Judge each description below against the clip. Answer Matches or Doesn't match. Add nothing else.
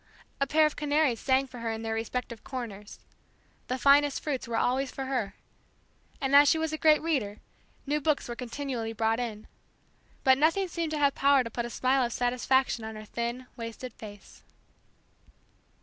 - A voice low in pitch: Doesn't match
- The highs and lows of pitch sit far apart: Doesn't match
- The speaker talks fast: Doesn't match